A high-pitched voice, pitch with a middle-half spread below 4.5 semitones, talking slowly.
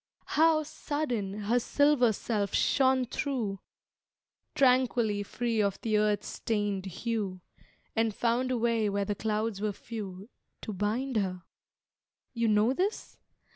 Yes: high, 225 Hz; average, 3.6 semitones; slow, 130 wpm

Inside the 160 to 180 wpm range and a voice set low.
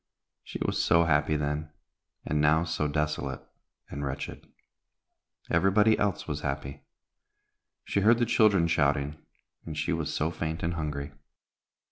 No: slow, 135 wpm; very low, 75 Hz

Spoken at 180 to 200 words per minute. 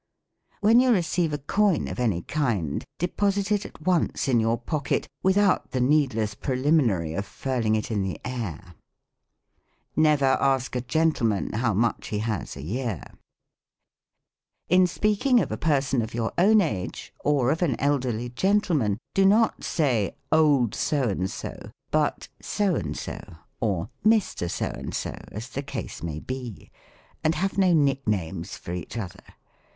No: average, 155 wpm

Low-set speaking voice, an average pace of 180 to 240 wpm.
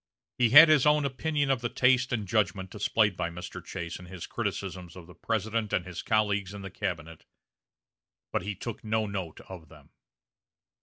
Yes: low, 100 Hz; average, 185 wpm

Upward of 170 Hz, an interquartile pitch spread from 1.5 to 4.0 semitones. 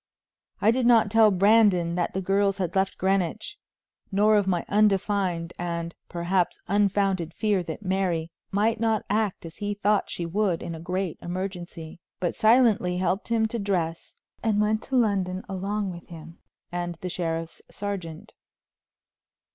Yes: high, 190 Hz; average, 3.2 semitones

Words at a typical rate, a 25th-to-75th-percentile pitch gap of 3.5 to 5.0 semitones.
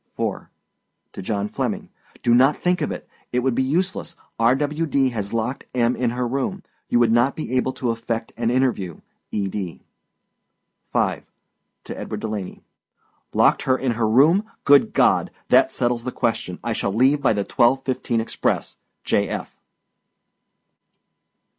No: average, 160 wpm; average, 2.9 semitones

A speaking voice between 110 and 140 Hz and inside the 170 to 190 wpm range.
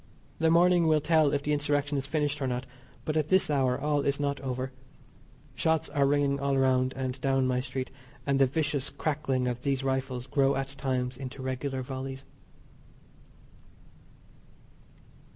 No: low, 135 Hz; average, 160 wpm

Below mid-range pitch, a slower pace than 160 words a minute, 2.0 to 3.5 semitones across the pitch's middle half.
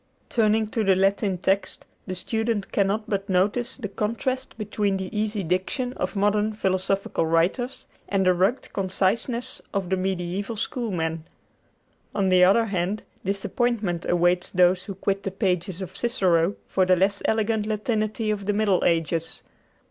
No: high, 195 Hz; average, 150 wpm; average, 2.7 semitones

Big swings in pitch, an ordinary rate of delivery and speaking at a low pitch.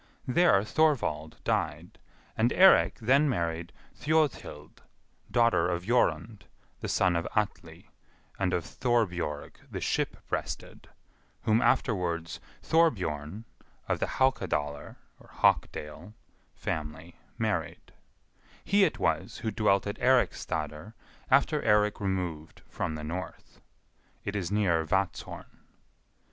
No: wide, 6.4 semitones; slow, 105 wpm; low, 100 Hz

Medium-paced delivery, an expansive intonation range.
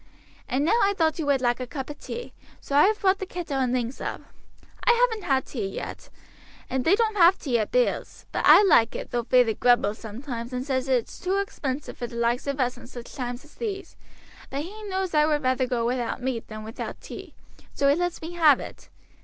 No: fast, 230 wpm; wide, 6.2 semitones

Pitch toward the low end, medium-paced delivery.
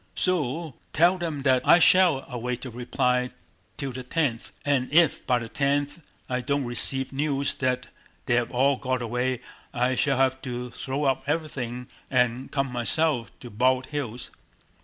Yes: low, 130 Hz; average, 160 wpm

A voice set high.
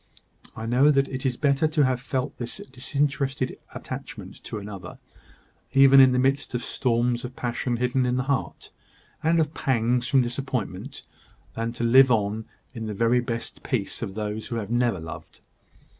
No: low, 125 Hz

